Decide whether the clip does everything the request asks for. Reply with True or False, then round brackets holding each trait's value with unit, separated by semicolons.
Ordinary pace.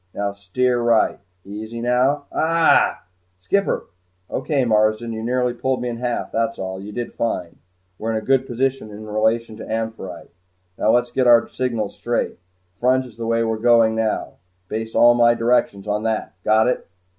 True (170 wpm)